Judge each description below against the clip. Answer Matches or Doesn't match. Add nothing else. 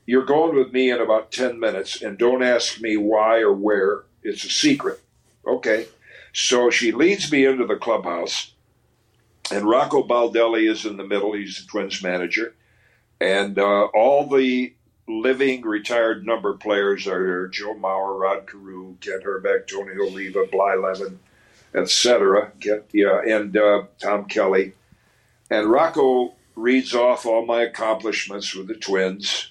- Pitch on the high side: Doesn't match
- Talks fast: Doesn't match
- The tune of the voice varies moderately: Matches